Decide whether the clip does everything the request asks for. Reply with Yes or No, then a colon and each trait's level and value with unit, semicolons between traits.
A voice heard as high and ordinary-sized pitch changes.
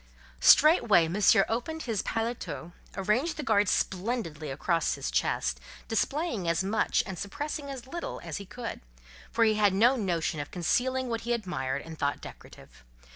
No: high, 210 Hz; wide, 5.8 semitones